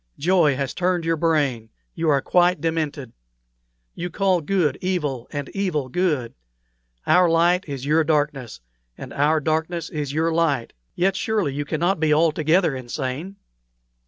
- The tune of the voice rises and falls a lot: No, average, 3.5 semitones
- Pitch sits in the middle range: Yes, medium, 160 Hz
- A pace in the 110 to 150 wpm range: Yes, average, 140 wpm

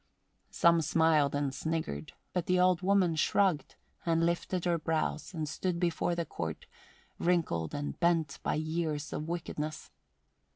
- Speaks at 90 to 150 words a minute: Yes, average, 140 wpm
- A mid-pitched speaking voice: Yes, medium, 165 Hz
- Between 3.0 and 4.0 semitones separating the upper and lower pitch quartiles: No, narrow, 2.4 semitones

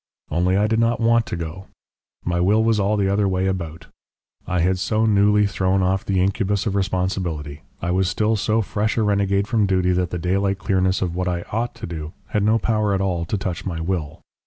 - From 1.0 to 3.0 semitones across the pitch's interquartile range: Yes, narrow, 2.6 semitones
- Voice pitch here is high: No, very low, 95 Hz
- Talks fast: Yes, fast, 220 wpm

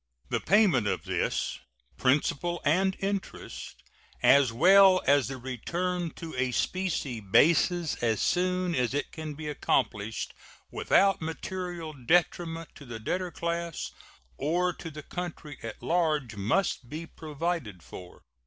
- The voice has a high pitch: No, medium, 160 Hz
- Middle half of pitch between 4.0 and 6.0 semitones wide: Yes, wide, 5.5 semitones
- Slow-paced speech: Yes, slow, 130 wpm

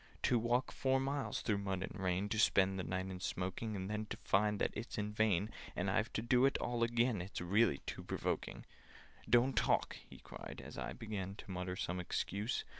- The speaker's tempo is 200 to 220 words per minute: Yes, fast, 205 wpm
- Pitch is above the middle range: No, low, 105 Hz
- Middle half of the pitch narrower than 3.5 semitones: No, average, 3.8 semitones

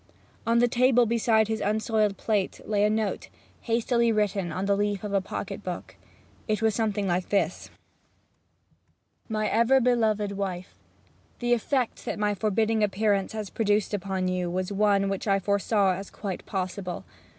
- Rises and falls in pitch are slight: Yes, narrow, 2.1 semitones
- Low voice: No, high, 210 Hz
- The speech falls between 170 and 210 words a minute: No, average, 160 wpm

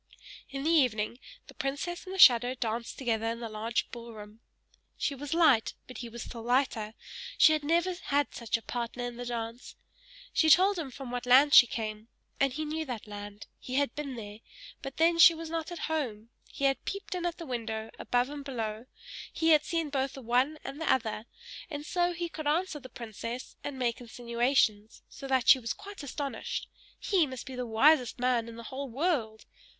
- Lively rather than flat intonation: No, average, 4.5 semitones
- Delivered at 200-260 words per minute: Yes, fast, 205 wpm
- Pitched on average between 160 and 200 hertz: No, very high, 255 Hz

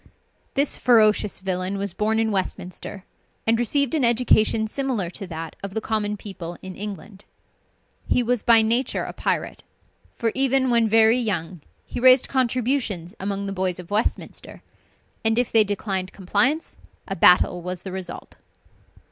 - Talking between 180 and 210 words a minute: No, average, 155 wpm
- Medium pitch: No, high, 210 Hz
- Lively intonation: No, average, 3.9 semitones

